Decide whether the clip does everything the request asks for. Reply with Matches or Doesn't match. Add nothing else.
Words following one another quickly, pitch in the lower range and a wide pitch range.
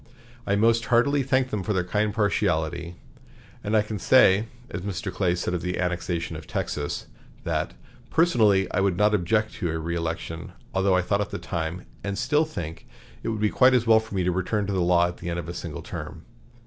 Doesn't match